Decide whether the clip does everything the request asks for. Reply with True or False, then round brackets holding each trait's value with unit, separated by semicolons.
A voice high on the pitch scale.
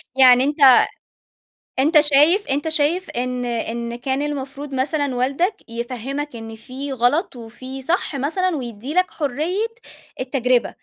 True (270 Hz)